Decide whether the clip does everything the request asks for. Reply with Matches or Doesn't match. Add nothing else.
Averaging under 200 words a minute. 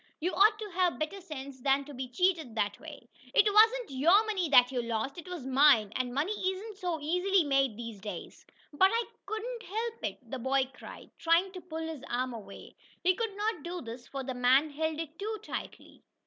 Doesn't match